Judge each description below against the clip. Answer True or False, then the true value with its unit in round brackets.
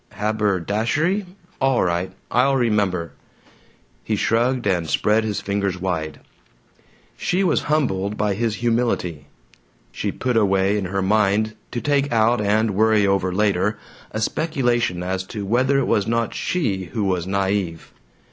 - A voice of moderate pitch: False (105 Hz)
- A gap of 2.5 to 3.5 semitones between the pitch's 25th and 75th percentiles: False (3.9 semitones)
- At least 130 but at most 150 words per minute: True (140 wpm)